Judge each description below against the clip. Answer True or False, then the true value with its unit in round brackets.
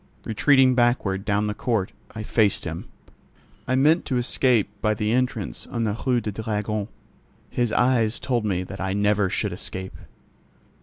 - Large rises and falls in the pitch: False (3.2 semitones)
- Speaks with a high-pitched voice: False (110 Hz)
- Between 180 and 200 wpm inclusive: False (160 wpm)